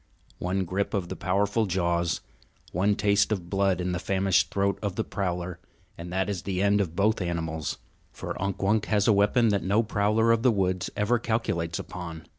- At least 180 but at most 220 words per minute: Yes, average, 195 wpm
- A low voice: Yes, very low, 95 Hz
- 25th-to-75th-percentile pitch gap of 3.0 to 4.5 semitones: No, narrow, 2.5 semitones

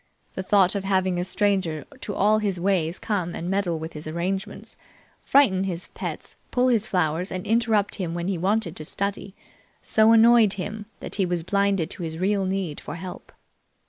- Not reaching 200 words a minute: Yes, average, 185 wpm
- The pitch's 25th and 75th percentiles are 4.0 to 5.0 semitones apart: No, average, 2.9 semitones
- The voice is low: No, high, 190 Hz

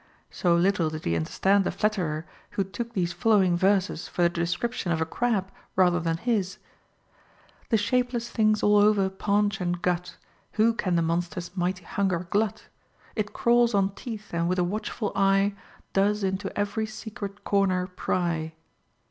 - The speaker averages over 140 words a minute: Yes, average, 165 wpm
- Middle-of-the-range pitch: No, high, 195 Hz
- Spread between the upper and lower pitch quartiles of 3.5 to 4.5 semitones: No, average, 3.1 semitones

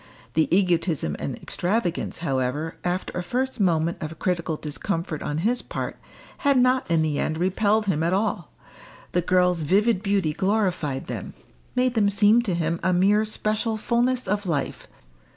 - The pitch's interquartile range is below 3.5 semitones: No, average, 4.6 semitones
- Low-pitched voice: No, medium, 185 Hz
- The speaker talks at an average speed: Yes, average, 160 wpm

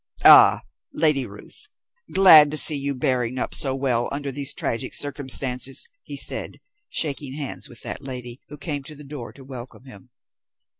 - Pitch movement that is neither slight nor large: No, narrow, 2.3 semitones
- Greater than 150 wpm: Yes, average, 165 wpm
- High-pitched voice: No, low, 135 Hz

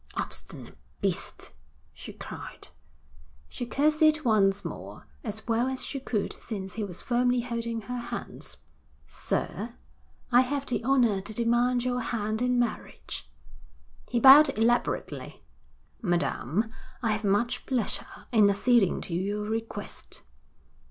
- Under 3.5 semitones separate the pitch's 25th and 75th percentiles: Yes, average, 2.9 semitones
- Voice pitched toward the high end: Yes, high, 235 Hz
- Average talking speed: No, slow, 125 wpm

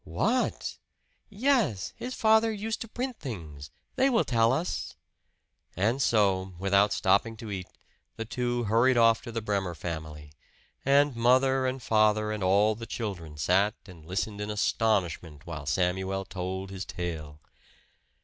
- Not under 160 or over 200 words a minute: No, average, 145 wpm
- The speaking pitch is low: Yes, low, 105 Hz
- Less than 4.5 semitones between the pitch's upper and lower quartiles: No, average, 5.2 semitones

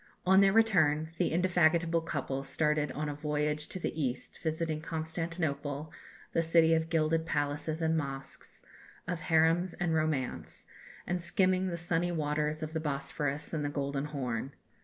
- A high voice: No, medium, 155 Hz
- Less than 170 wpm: Yes, average, 155 wpm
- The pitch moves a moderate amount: No, narrow, 2.1 semitones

